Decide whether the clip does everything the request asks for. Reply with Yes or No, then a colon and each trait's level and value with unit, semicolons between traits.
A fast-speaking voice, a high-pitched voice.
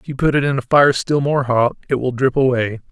No: fast, 290 wpm; low, 130 Hz